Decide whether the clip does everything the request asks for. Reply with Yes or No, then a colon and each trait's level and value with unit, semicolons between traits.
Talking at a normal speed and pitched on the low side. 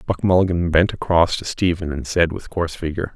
No: fast, 210 wpm; very low, 85 Hz